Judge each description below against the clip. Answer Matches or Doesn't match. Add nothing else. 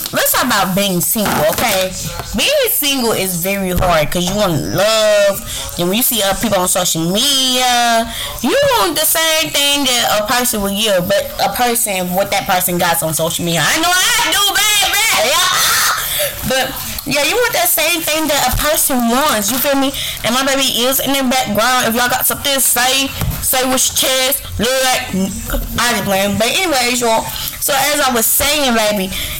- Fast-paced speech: Doesn't match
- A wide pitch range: Matches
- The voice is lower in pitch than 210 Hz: Doesn't match